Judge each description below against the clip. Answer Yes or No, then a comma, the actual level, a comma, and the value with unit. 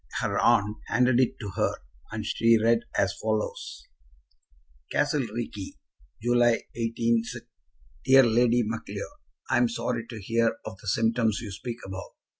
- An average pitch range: No, narrow, 1.8 semitones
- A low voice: Yes, low, 115 Hz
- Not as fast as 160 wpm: Yes, average, 140 wpm